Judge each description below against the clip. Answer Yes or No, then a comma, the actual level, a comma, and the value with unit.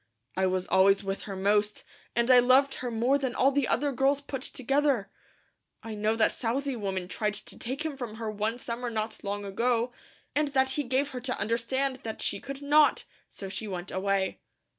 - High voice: Yes, high, 235 Hz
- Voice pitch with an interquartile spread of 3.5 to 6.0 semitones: Yes, average, 4.5 semitones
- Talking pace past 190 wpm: Yes, average, 200 wpm